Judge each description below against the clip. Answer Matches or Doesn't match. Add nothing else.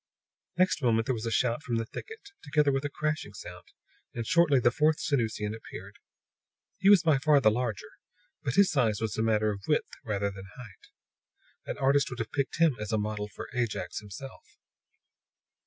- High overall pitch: Doesn't match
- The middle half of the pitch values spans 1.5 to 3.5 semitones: Doesn't match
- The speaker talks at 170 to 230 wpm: Matches